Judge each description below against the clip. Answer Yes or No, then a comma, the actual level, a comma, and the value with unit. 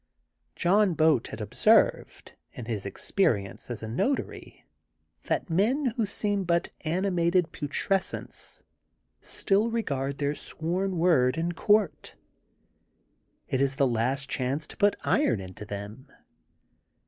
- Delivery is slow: Yes, slow, 125 wpm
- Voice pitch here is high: No, medium, 160 Hz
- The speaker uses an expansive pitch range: Yes, wide, 7.3 semitones